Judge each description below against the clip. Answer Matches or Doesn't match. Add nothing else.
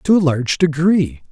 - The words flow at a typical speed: Matches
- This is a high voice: Doesn't match